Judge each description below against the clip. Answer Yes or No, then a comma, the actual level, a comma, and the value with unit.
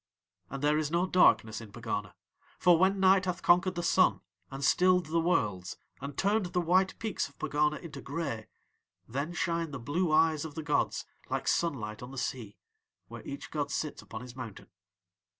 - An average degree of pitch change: Yes, average, 4.8 semitones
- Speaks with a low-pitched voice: No, medium, 155 Hz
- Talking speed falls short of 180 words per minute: No, average, 185 wpm